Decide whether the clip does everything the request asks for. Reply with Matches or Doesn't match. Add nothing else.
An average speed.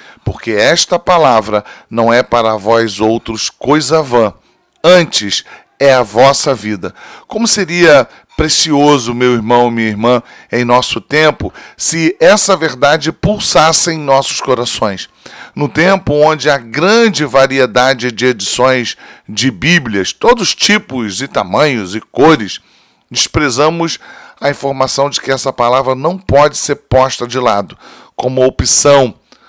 Matches